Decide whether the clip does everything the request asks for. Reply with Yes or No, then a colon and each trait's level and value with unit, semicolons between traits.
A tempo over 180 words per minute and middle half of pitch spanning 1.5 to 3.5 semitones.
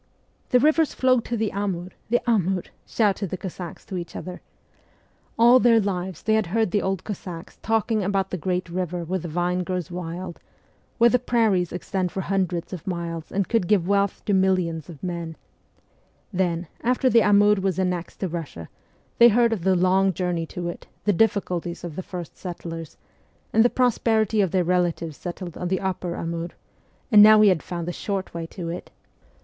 Yes: average, 190 wpm; average, 3.1 semitones